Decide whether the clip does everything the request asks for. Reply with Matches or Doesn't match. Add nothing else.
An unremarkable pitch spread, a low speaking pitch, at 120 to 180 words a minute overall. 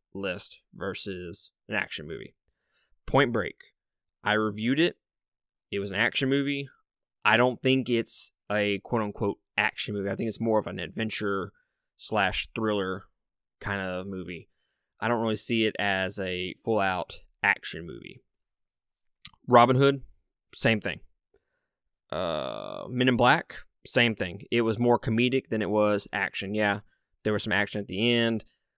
Matches